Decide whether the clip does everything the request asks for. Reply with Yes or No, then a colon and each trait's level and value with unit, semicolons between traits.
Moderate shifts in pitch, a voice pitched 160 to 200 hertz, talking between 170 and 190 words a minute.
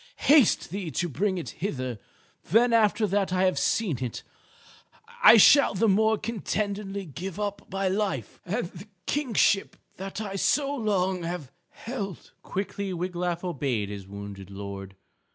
No: average, 4.4 semitones; high, 190 Hz; average, 145 wpm